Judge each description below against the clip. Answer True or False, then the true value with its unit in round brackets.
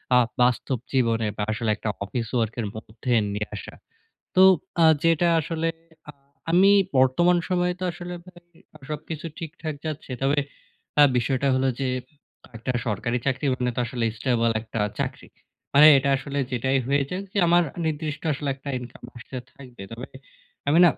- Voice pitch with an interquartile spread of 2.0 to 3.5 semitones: False (4.8 semitones)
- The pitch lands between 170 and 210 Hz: False (135 Hz)